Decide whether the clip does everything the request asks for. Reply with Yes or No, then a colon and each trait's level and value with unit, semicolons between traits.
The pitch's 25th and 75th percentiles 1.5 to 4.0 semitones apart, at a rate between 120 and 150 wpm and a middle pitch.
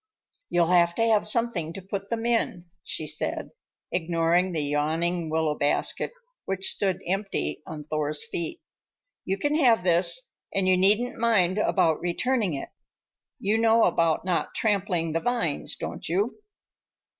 No: average, 4.5 semitones; average, 145 wpm; medium, 180 Hz